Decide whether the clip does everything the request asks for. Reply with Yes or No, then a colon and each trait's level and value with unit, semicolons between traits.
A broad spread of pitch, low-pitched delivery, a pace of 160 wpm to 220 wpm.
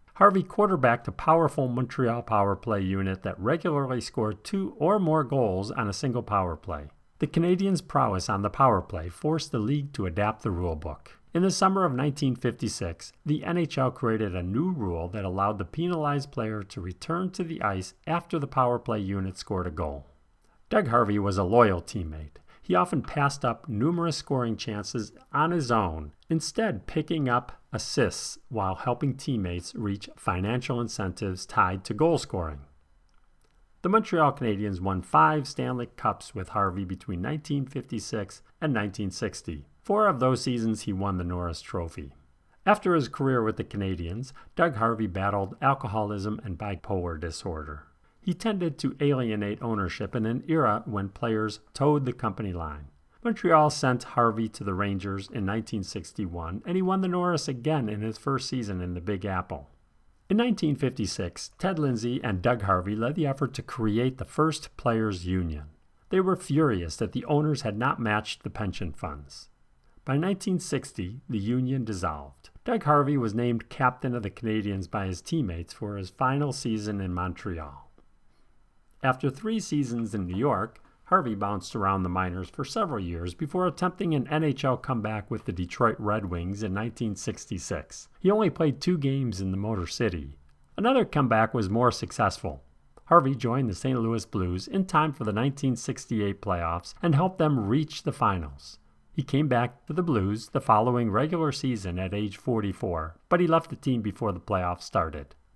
Yes: wide, 6.8 semitones; low, 115 Hz; average, 165 wpm